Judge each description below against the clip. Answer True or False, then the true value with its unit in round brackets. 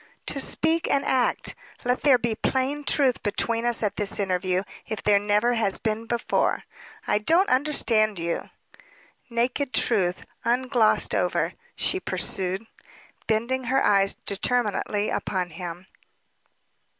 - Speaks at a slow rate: True (125 wpm)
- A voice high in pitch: True (225 Hz)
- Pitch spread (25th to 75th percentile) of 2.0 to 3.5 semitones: False (4.1 semitones)